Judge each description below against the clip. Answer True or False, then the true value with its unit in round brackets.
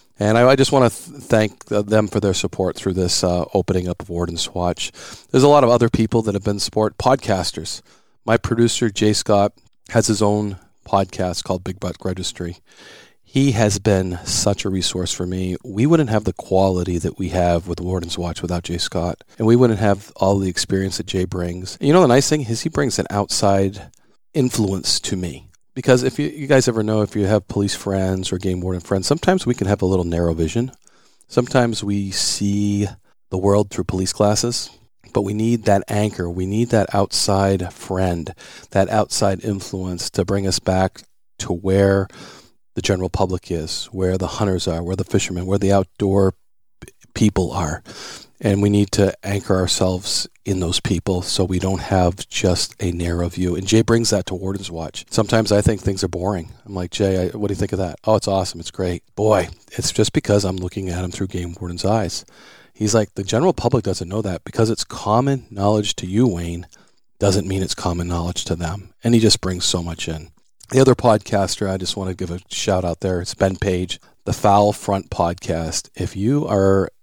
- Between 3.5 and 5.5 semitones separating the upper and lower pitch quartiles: False (2.9 semitones)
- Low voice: True (100 Hz)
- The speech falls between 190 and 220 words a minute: True (205 wpm)